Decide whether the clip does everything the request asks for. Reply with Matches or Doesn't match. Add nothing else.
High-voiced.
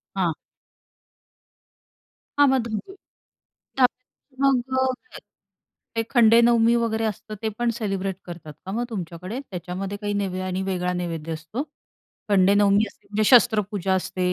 Matches